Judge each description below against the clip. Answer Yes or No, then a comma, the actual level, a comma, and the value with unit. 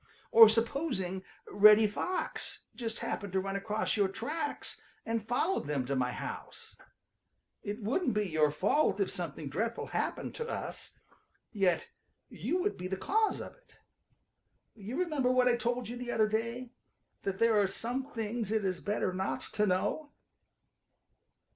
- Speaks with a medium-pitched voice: No, high, 220 Hz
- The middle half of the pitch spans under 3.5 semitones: No, average, 4.3 semitones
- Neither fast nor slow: Yes, average, 155 wpm